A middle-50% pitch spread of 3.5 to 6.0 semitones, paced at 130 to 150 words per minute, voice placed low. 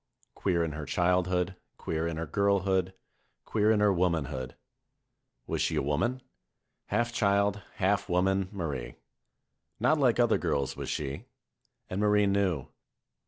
Yes: average, 3.8 semitones; slow, 135 wpm; very low, 95 Hz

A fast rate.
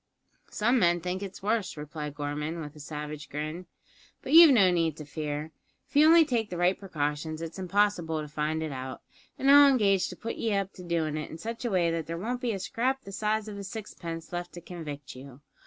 Yes: fast, 225 wpm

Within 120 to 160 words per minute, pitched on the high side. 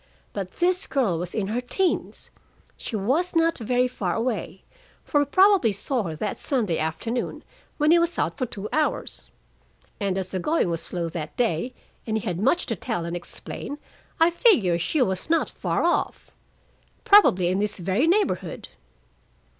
No: average, 170 wpm; high, 225 Hz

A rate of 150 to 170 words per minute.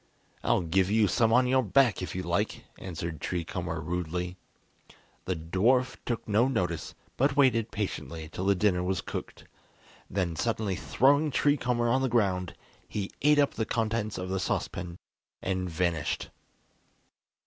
Yes: average, 155 wpm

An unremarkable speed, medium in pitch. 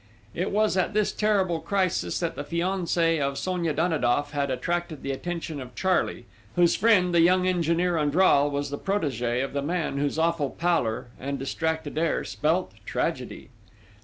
Yes: average, 160 wpm; medium, 165 Hz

